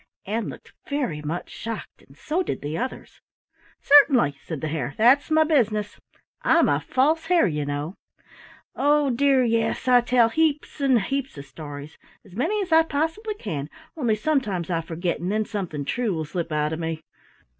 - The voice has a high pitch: Yes, high, 225 Hz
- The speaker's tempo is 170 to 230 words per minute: Yes, average, 175 wpm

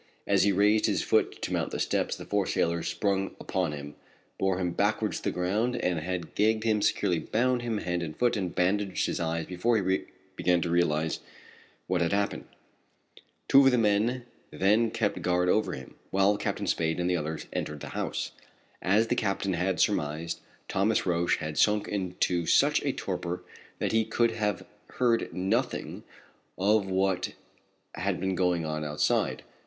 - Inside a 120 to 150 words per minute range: No, average, 175 wpm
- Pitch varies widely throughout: No, average, 3.6 semitones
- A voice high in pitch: No, very low, 95 Hz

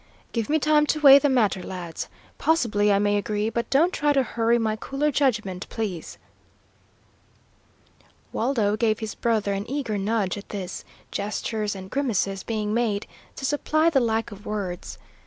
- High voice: Yes, high, 220 Hz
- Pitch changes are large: No, average, 4.7 semitones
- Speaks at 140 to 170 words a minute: Yes, average, 160 wpm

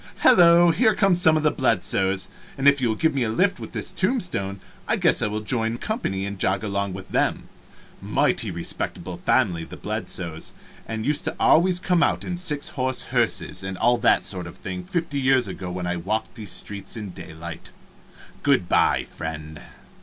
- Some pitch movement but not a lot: No, wide, 8.4 semitones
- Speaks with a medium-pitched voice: No, low, 110 Hz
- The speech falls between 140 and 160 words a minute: No, average, 190 wpm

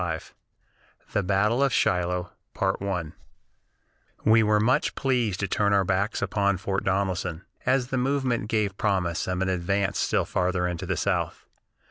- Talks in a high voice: No, low, 100 Hz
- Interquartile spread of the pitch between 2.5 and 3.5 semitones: Yes, average, 3.0 semitones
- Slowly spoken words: No, average, 145 wpm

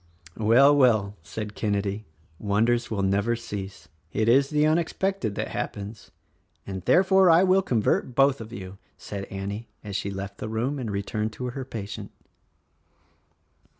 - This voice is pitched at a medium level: No, low, 110 Hz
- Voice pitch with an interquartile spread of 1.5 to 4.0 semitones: No, average, 4.6 semitones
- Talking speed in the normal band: Yes, average, 160 wpm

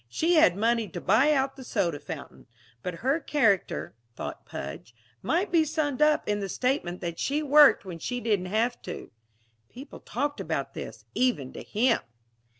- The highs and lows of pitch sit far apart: Yes, wide, 8.1 semitones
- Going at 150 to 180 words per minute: Yes, average, 170 wpm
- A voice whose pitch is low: No, high, 235 Hz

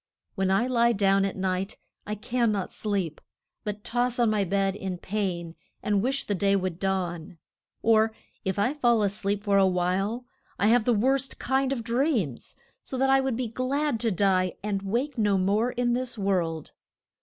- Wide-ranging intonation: No, average, 4.1 semitones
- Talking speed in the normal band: Yes, average, 190 wpm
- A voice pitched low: No, high, 210 Hz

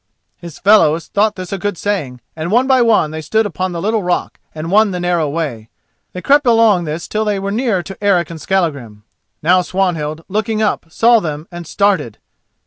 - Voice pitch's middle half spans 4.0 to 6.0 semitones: Yes, average, 4.6 semitones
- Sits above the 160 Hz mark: Yes, medium, 185 Hz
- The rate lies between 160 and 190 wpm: No, average, 200 wpm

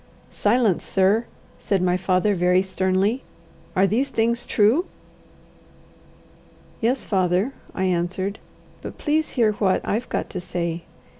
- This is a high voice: Yes, high, 195 Hz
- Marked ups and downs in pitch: No, average, 4.0 semitones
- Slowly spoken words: Yes, slow, 125 wpm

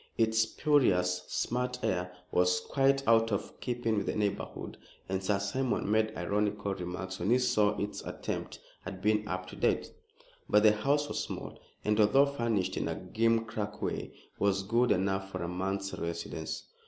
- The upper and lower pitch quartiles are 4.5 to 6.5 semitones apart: No, average, 3.2 semitones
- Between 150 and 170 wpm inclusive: Yes, average, 165 wpm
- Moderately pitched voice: No, low, 105 Hz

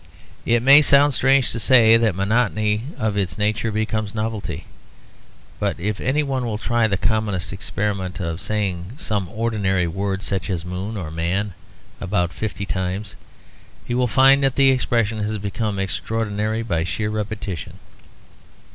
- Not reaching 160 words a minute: Yes, average, 150 wpm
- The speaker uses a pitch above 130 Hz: No, low, 105 Hz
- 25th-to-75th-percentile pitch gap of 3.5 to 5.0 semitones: No, average, 2.9 semitones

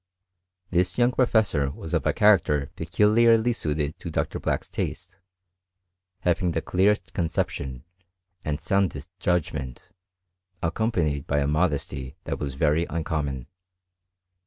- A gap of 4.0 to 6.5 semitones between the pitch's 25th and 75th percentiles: Yes, average, 5.2 semitones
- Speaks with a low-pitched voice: Yes, very low, 80 Hz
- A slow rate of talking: Yes, slow, 115 wpm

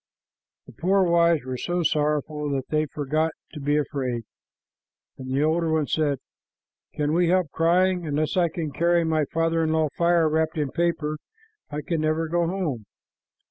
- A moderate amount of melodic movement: No, narrow, 2.3 semitones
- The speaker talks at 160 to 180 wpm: Yes, average, 175 wpm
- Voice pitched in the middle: Yes, medium, 160 Hz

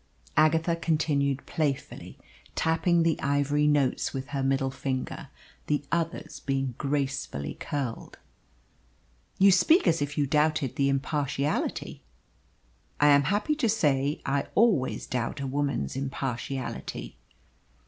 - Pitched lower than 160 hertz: Yes, medium, 140 Hz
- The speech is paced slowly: Yes, slow, 120 wpm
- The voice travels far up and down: No, narrow, 2.6 semitones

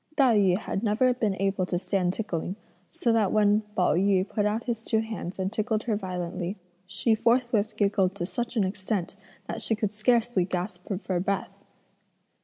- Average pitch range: Yes, average, 3.1 semitones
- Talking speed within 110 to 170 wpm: No, average, 180 wpm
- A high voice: Yes, high, 205 Hz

